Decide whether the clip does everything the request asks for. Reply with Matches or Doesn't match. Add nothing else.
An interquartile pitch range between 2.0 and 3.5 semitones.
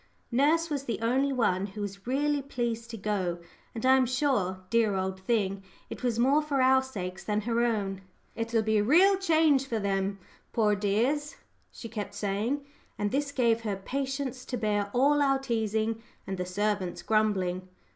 Doesn't match